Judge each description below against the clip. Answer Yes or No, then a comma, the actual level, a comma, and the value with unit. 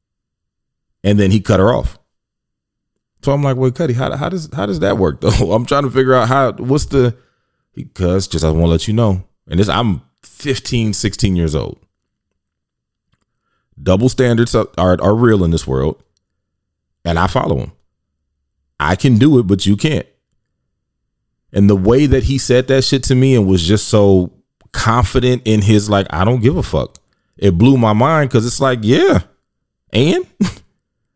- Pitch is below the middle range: Yes, low, 105 Hz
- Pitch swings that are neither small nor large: No, wide, 5.7 semitones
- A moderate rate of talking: Yes, average, 180 wpm